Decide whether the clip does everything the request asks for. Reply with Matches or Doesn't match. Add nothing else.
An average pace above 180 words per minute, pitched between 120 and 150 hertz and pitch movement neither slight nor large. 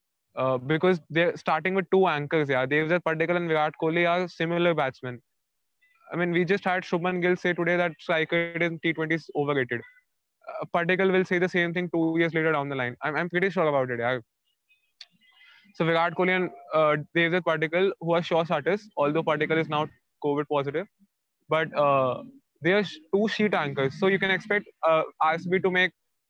Doesn't match